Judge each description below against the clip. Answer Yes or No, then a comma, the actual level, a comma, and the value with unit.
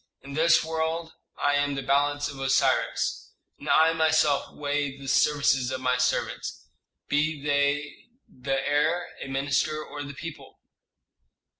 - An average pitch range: No, narrow, 2.0 semitones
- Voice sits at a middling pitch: Yes, medium, 145 Hz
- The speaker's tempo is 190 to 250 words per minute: No, average, 140 wpm